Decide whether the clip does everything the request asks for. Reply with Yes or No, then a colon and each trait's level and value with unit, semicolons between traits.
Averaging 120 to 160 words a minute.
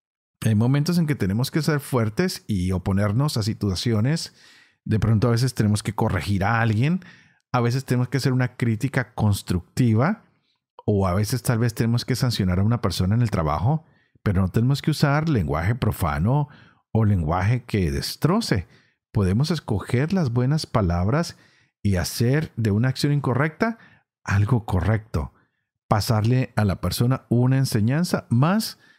Yes: average, 155 wpm